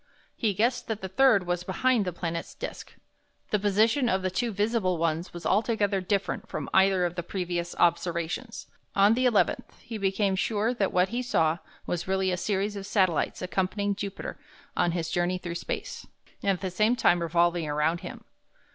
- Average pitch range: Yes, average, 3.3 semitones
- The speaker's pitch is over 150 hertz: Yes, high, 190 Hz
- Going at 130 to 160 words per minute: No, average, 180 wpm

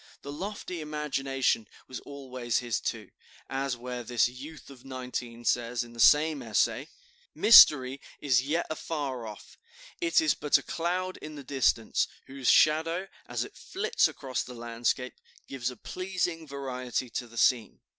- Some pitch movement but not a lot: Yes, average, 3.9 semitones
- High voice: No, low, 135 Hz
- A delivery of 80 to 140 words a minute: No, average, 155 wpm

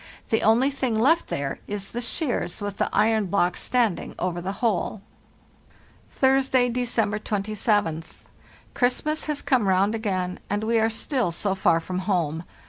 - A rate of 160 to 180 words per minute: No, average, 150 wpm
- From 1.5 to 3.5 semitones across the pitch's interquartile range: No, average, 4.7 semitones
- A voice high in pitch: Yes, high, 215 Hz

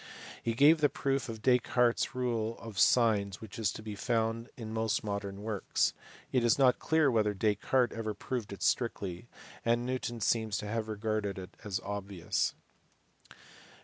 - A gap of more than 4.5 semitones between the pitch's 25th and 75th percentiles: No, average, 2.7 semitones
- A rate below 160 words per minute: No, average, 165 wpm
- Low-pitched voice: Yes, low, 110 Hz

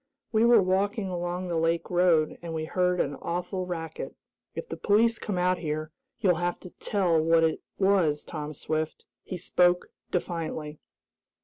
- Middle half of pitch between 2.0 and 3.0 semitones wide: Yes, narrow, 2.5 semitones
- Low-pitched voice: No, medium, 175 Hz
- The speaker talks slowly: No, average, 165 wpm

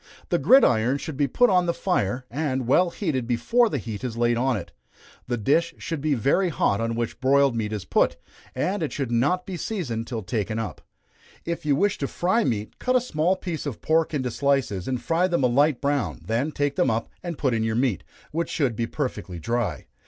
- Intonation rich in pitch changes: Yes, wide, 6.1 semitones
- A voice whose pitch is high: No, low, 135 Hz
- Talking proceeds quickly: Yes, fast, 220 wpm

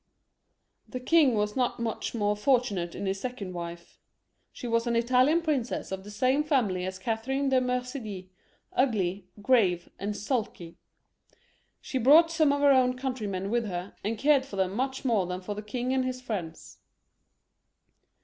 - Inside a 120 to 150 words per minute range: No, average, 170 wpm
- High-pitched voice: Yes, high, 235 Hz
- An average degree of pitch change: Yes, average, 4.9 semitones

